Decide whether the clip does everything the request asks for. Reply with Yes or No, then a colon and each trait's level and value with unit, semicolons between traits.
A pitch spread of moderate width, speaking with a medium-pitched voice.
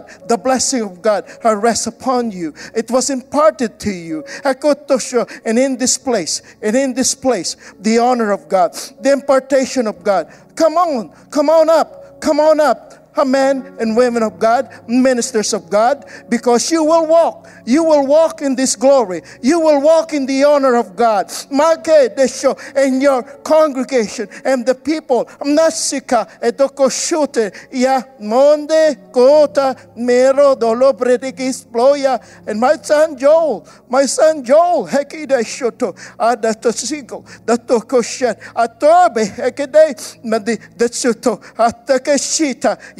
No: average, 3.6 semitones; very high, 265 Hz